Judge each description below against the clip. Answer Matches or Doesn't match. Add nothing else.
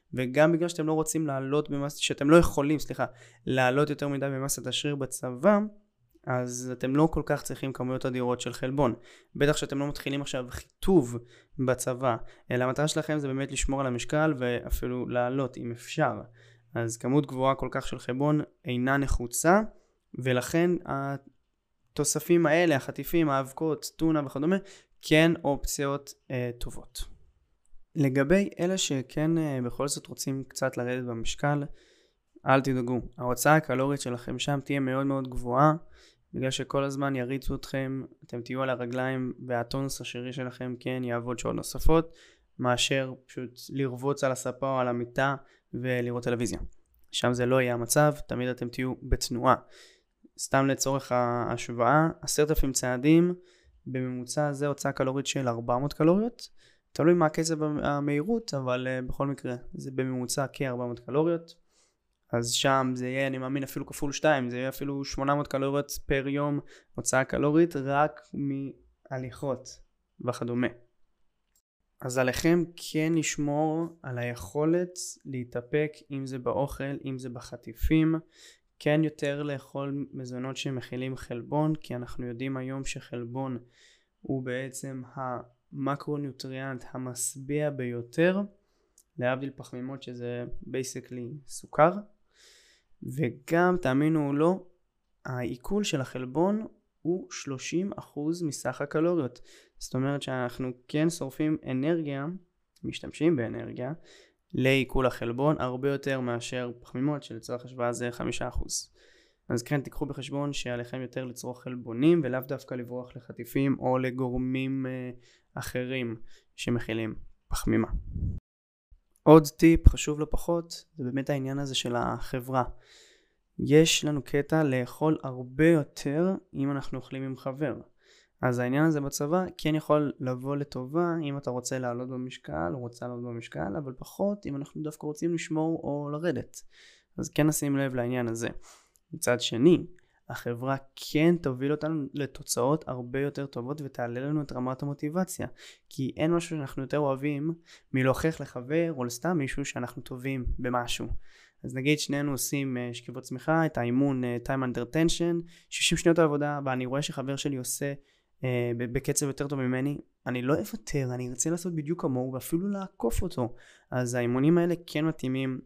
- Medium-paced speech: Matches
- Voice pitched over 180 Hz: Doesn't match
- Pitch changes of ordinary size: Matches